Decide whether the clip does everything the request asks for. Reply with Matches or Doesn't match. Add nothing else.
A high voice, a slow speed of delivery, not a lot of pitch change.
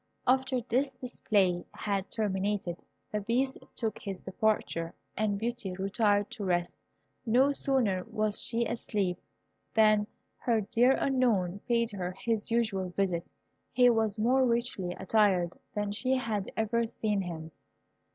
Doesn't match